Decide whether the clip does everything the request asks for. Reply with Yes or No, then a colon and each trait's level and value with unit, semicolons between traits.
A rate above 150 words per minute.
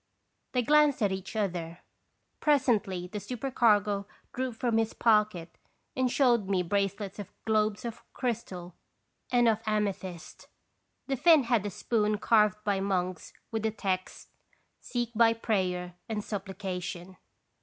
No: average, 140 wpm